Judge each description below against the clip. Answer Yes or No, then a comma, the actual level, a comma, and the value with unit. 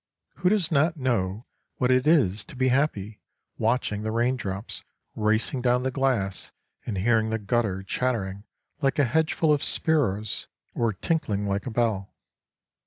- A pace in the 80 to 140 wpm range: No, average, 155 wpm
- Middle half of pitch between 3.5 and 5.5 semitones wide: Yes, average, 4.6 semitones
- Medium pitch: No, low, 120 Hz